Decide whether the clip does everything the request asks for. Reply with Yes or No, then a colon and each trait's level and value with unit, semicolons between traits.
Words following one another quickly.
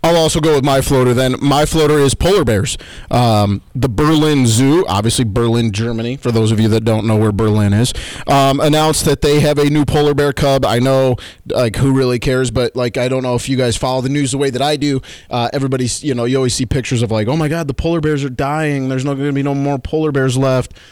Yes: fast, 255 wpm